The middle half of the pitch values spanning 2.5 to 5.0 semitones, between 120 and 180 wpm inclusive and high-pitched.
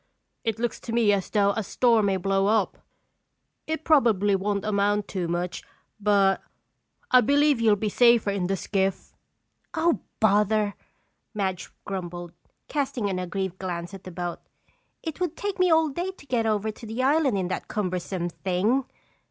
Yes: average, 4.1 semitones; average, 165 wpm; high, 205 Hz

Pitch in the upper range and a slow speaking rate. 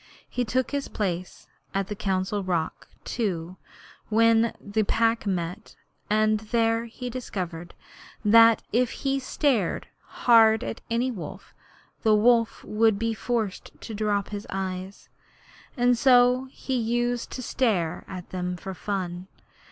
Yes: high, 220 Hz; slow, 130 wpm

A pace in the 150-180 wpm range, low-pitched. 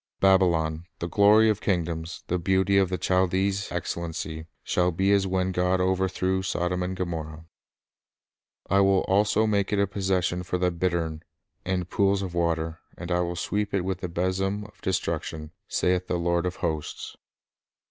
Yes: average, 170 wpm; very low, 90 Hz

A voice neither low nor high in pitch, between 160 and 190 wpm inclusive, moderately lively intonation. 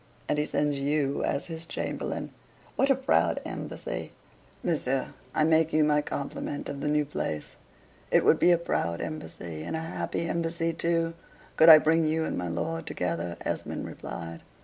Yes: medium, 155 Hz; average, 170 wpm; average, 3.0 semitones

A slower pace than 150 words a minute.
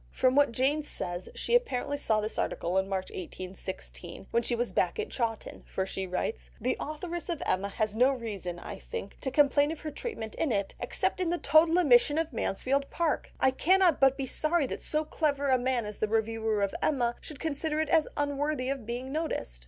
No: fast, 205 wpm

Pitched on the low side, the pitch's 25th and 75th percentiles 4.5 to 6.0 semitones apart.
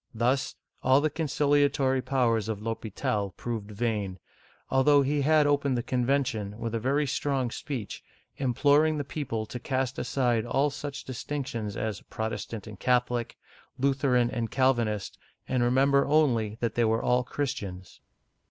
No: low, 125 Hz; average, 3.7 semitones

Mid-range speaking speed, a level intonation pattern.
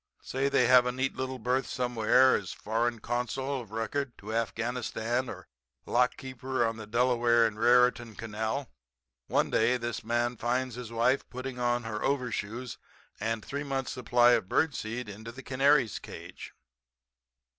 Yes: average, 155 wpm; narrow, 2.1 semitones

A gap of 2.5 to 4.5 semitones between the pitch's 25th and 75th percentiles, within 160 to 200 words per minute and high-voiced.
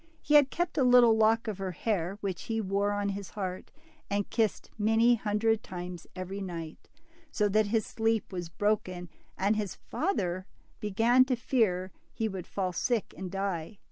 Yes: average, 3.2 semitones; average, 170 wpm; high, 205 Hz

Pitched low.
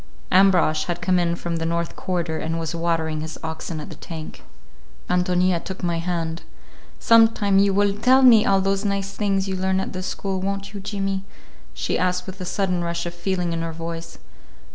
No: medium, 180 Hz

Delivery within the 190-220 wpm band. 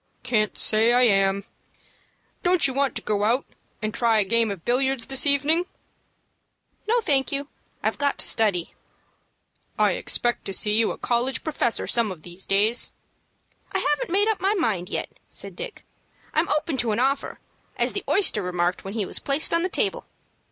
No: average, 180 wpm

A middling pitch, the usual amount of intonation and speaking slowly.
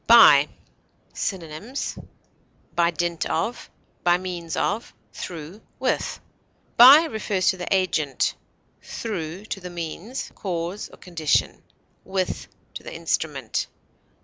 Yes: medium, 180 Hz; average, 3.6 semitones; slow, 110 wpm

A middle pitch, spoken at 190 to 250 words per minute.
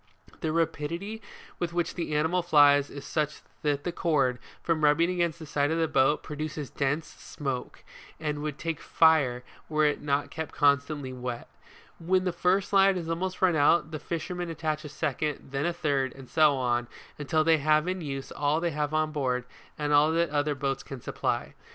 Yes: medium, 155 Hz; average, 195 wpm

